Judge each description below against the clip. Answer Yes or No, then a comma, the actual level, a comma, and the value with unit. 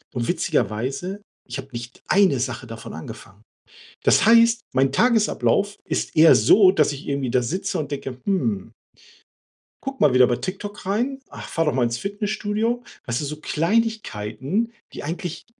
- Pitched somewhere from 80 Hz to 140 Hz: No, medium, 160 Hz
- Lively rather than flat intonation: Yes, wide, 8.4 semitones